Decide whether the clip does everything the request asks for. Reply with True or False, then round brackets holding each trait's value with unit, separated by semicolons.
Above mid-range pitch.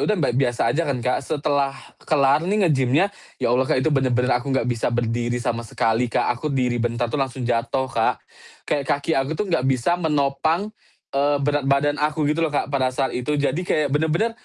False (140 Hz)